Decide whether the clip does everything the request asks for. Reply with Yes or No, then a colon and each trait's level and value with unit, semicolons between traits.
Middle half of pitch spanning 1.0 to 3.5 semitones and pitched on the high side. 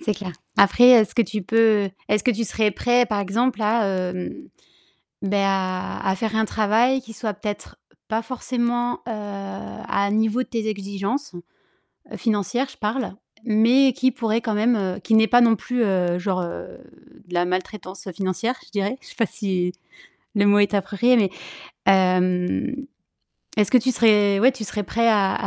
Yes: average, 3.1 semitones; high, 215 Hz